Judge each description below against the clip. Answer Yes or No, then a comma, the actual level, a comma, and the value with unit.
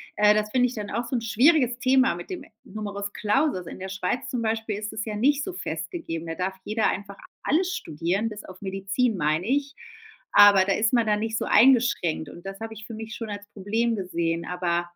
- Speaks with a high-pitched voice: Yes, high, 210 Hz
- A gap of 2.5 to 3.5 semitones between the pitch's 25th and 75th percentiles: No, average, 3.9 semitones